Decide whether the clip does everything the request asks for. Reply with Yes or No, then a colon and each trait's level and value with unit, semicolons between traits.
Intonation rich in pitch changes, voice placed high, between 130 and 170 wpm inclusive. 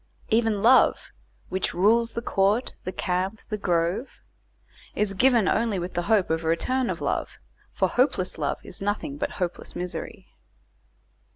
No: average, 4.5 semitones; high, 200 Hz; average, 155 wpm